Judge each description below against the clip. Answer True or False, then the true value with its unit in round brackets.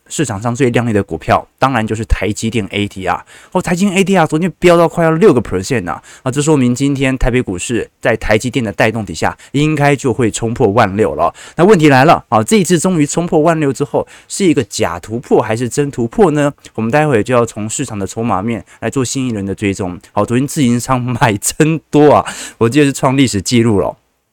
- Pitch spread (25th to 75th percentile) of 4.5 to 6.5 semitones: True (5.1 semitones)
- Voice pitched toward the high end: False (125 Hz)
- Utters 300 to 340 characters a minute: False (350 characters per minute)